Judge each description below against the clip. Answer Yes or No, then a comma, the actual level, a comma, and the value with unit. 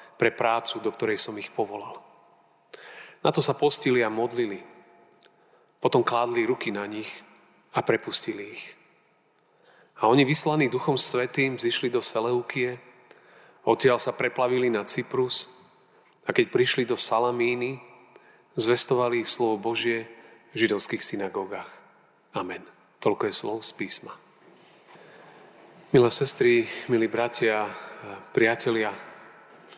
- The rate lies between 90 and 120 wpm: Yes, average, 115 wpm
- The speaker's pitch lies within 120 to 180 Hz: Yes, low, 125 Hz